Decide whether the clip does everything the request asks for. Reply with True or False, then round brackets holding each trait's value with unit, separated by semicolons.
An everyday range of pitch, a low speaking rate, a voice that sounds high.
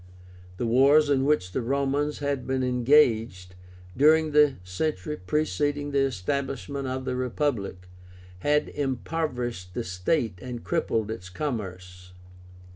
False (5.0 semitones; 120 wpm; 130 Hz)